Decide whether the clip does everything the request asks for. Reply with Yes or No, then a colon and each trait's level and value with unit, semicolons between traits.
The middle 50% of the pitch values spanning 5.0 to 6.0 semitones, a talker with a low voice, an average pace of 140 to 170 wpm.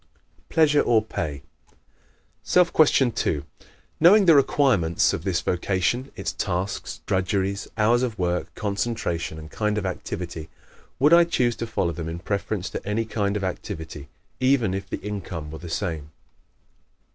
Yes: wide, 5.6 semitones; low, 100 Hz; average, 155 wpm